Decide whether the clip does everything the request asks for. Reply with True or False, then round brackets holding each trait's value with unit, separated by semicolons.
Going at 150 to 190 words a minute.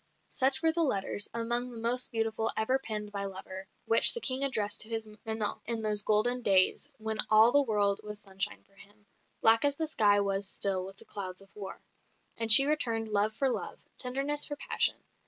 False (200 wpm)